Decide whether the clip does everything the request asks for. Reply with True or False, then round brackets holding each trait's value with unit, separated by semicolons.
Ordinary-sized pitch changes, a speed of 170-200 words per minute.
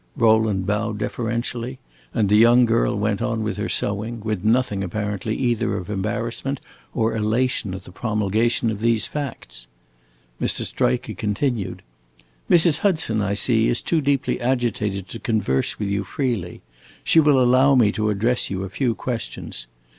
False (3.1 semitones; 155 wpm)